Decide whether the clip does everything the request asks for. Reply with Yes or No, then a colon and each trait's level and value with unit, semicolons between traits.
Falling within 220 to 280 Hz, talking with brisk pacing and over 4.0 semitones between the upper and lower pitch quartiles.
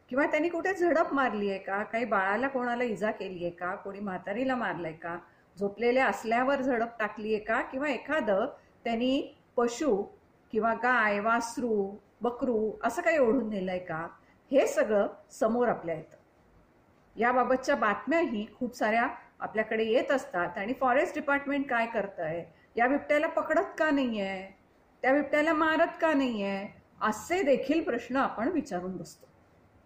Yes: high, 235 Hz; fast, 140 wpm; wide, 5.6 semitones